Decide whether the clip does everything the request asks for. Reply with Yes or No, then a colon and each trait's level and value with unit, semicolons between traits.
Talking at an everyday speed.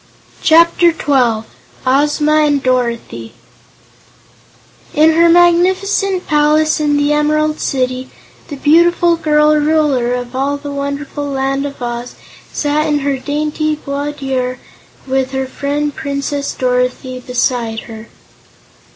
No: slow, 115 wpm